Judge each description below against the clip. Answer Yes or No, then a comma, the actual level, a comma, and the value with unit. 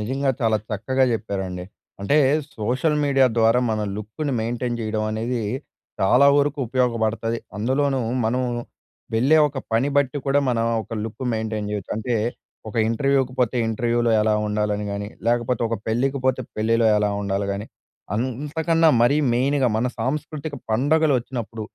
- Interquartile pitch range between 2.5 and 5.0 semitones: Yes, average, 3.6 semitones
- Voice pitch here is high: No, low, 120 Hz